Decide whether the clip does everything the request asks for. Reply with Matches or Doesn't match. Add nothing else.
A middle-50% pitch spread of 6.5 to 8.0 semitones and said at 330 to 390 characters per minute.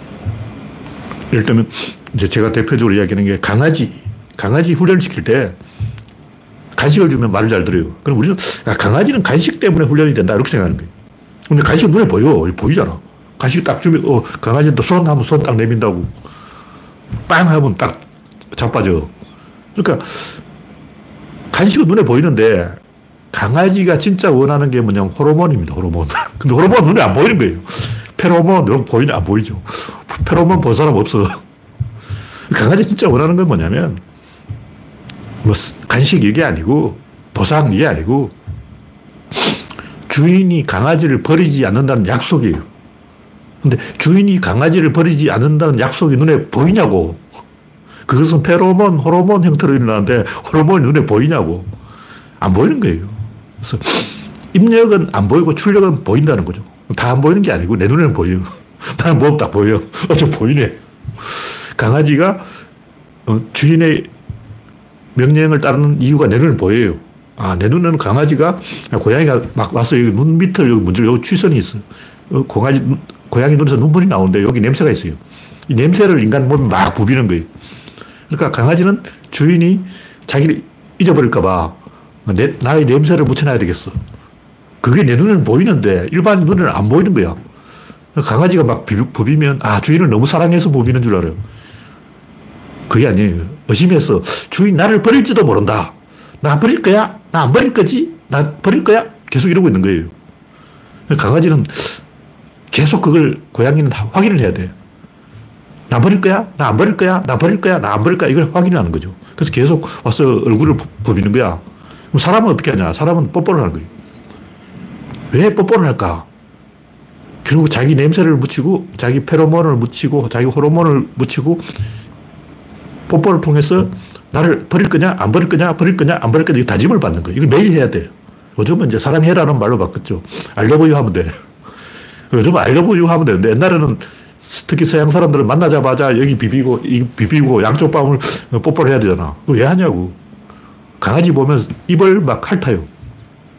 Matches